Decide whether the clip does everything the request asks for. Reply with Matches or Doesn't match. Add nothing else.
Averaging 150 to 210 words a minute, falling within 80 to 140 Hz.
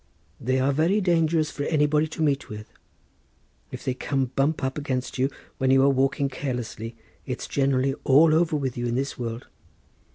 Matches